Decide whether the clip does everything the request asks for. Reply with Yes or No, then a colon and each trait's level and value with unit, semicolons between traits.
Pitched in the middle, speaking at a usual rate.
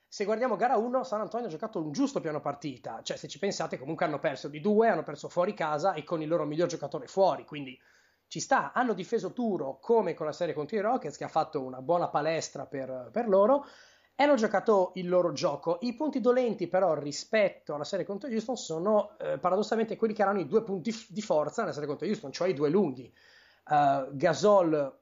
No: medium, 180 Hz; fast, 220 wpm